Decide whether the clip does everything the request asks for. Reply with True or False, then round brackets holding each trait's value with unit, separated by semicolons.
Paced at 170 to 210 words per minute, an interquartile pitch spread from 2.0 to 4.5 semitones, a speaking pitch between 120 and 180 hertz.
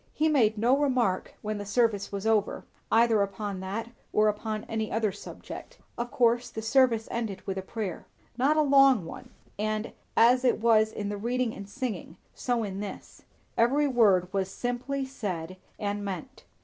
False (175 wpm; 3.5 semitones; 220 Hz)